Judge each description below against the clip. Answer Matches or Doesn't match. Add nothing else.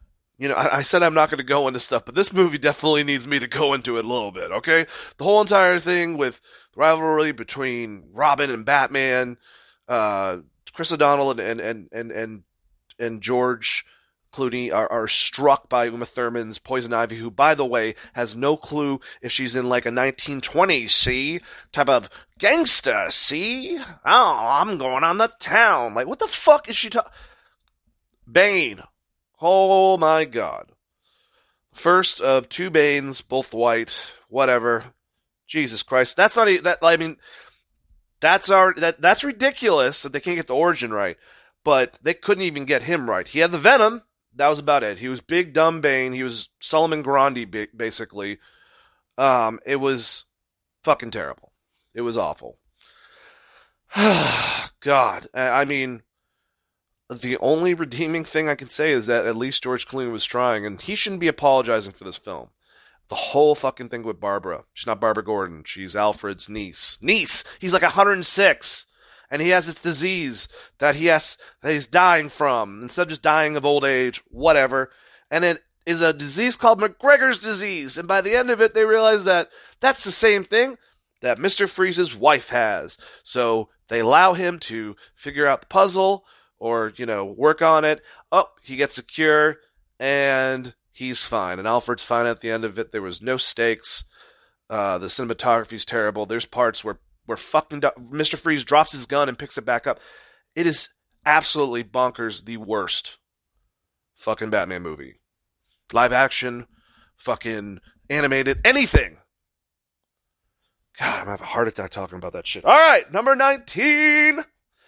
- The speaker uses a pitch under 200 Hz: Matches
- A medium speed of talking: Matches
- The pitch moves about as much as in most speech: Doesn't match